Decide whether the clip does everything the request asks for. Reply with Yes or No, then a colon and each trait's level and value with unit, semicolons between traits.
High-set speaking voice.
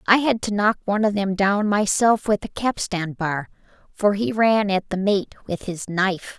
Yes: high, 200 Hz